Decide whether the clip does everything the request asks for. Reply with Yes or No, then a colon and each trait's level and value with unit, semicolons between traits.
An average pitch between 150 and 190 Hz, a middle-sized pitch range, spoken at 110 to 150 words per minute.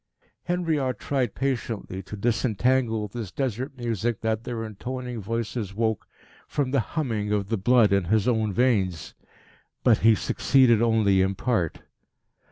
No: low, 115 Hz; average, 3.4 semitones; average, 140 wpm